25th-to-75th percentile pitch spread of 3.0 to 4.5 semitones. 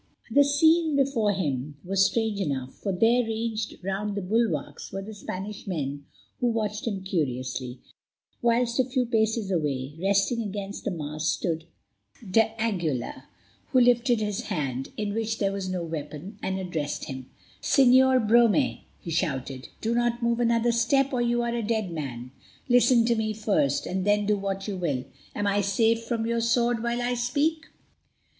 No: average, 5.1 semitones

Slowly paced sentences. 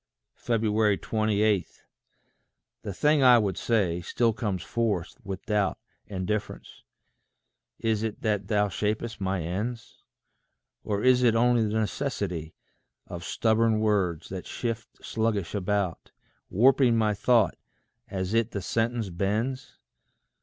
Yes: slow, 120 wpm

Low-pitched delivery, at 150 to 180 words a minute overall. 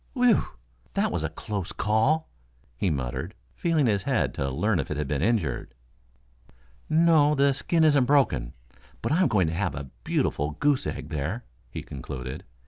Yes: low, 100 Hz; average, 165 wpm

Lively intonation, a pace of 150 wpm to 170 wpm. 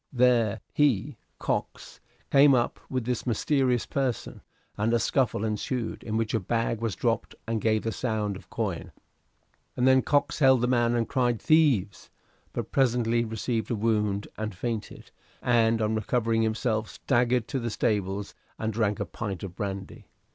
No: narrow, 2.4 semitones; average, 160 wpm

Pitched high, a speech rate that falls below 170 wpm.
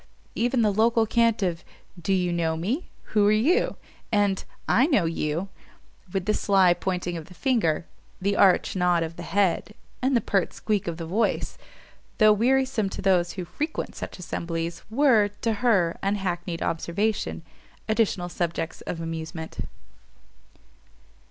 Yes: high, 195 Hz; average, 150 wpm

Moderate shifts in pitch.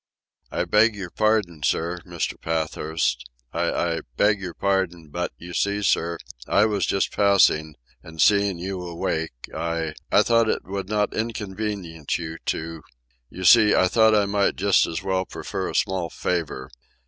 Yes: average, 3.7 semitones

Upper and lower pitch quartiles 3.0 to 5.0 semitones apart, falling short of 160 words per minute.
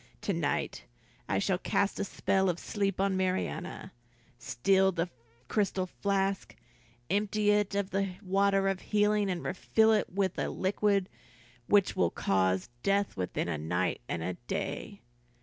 No: narrow, 2.4 semitones; average, 150 wpm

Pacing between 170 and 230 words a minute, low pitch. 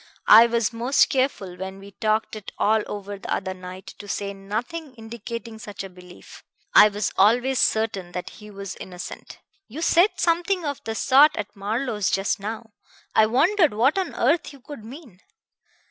No: average, 175 wpm; high, 220 Hz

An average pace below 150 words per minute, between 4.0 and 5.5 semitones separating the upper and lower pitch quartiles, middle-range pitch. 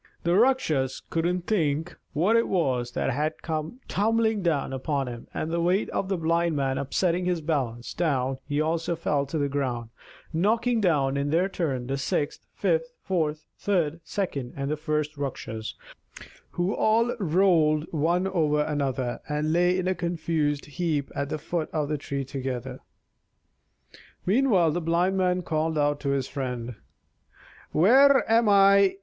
No: average, 155 wpm; average, 4.4 semitones; medium, 160 Hz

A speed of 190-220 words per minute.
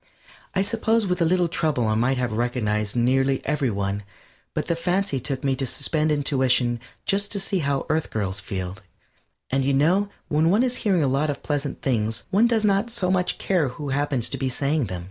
Yes: fast, 205 wpm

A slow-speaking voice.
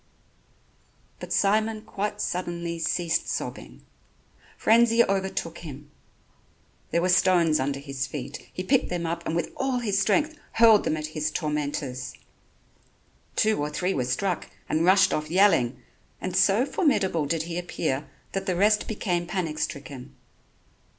No: average, 145 wpm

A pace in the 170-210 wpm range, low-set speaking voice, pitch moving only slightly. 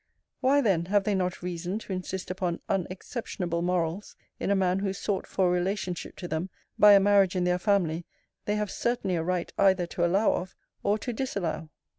No: average, 190 wpm; medium, 185 Hz; narrow, 2.3 semitones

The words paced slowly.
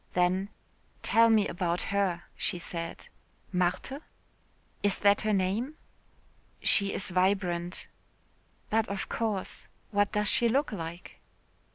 Yes: slow, 115 wpm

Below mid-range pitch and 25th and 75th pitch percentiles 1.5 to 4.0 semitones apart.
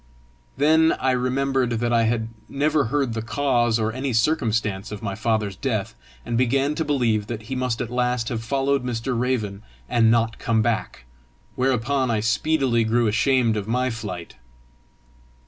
Yes: low, 120 Hz; average, 3.0 semitones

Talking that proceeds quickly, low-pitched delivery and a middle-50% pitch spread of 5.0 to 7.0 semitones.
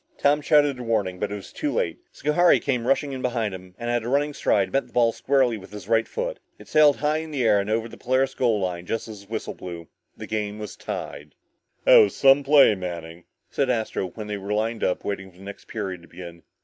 Yes: fast, 240 wpm; low, 115 Hz; wide, 5.6 semitones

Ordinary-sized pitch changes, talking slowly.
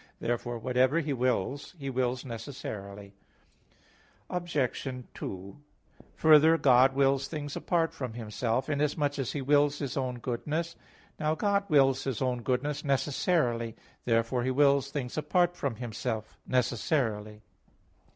Yes: average, 3.5 semitones; slow, 125 wpm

